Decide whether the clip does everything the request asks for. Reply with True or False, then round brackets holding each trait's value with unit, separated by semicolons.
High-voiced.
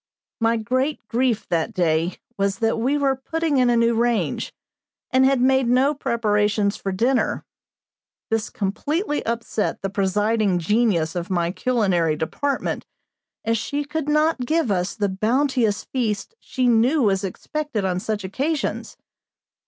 True (230 Hz)